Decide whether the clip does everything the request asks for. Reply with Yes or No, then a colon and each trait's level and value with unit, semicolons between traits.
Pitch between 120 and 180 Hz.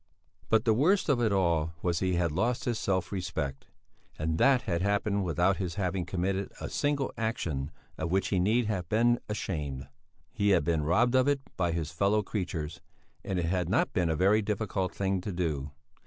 No: very low, 95 Hz